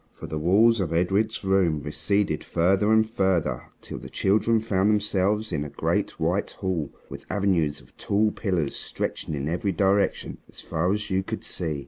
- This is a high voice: No, very low, 95 Hz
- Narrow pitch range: No, average, 4.0 semitones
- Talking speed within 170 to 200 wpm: Yes, average, 175 wpm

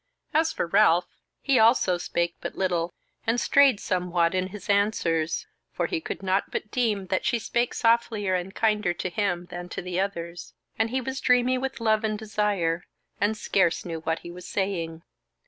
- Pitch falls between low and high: No, high, 195 Hz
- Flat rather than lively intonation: No, average, 4.2 semitones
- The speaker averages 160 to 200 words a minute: Yes, average, 180 wpm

